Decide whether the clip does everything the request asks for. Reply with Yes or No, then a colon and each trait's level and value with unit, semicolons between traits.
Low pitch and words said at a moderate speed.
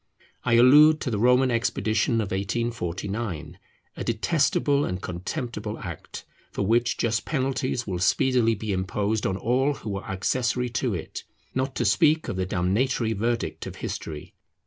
Yes: low, 115 Hz; average, 150 wpm